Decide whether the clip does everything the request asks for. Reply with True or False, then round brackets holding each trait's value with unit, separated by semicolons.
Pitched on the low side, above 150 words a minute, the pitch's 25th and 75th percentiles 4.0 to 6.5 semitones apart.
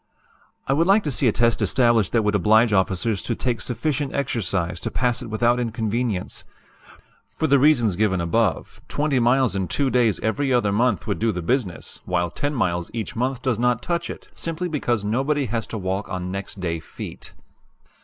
True (115 Hz; 190 wpm; 4.6 semitones)